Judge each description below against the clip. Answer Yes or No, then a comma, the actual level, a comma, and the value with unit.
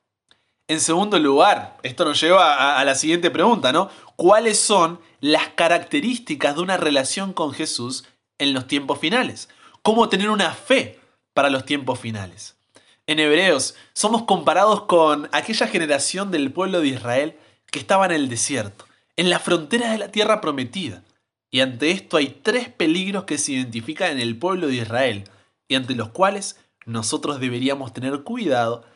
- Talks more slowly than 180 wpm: Yes, average, 160 wpm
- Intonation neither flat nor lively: No, wide, 6.7 semitones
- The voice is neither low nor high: Yes, medium, 155 Hz